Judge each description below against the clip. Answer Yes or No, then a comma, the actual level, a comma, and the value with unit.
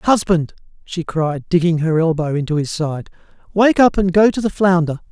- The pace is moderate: Yes, average, 190 wpm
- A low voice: No, medium, 175 Hz